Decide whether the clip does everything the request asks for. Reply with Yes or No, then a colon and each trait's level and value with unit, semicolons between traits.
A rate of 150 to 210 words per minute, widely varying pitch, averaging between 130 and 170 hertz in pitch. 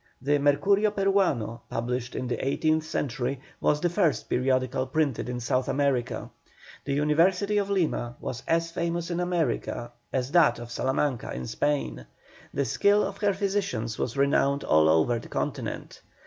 Yes: average, 155 wpm; wide, 6.0 semitones; medium, 140 Hz